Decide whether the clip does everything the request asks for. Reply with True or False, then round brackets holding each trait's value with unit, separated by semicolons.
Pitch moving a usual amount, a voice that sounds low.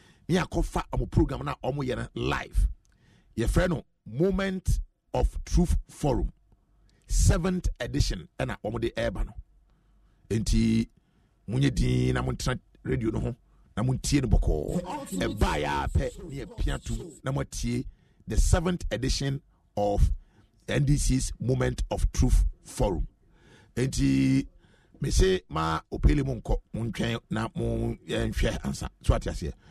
False (5.7 semitones; 115 Hz)